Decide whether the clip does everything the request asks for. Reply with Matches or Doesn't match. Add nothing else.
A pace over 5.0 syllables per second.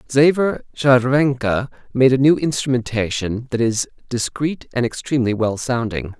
Doesn't match